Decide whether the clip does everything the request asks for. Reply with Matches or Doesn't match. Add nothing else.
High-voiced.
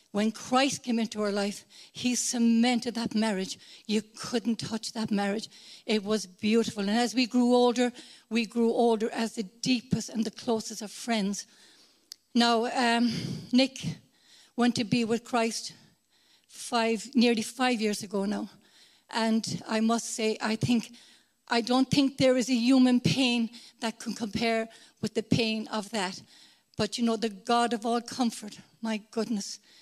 Matches